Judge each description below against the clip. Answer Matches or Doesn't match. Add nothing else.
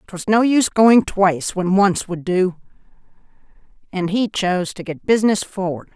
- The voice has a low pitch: Doesn't match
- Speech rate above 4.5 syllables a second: Matches